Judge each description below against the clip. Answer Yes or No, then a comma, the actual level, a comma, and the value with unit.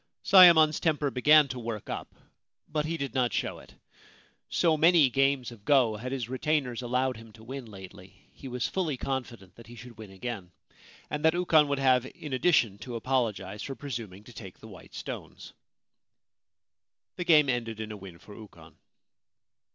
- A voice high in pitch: No, low, 125 Hz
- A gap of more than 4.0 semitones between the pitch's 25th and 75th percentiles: Yes, average, 4.7 semitones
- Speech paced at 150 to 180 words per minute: Yes, average, 175 wpm